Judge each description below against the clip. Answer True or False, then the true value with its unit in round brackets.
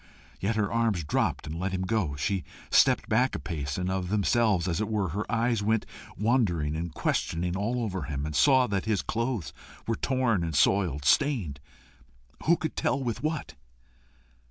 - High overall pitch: False (100 Hz)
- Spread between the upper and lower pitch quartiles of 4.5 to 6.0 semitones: True (5.5 semitones)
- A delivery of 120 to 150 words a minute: False (180 wpm)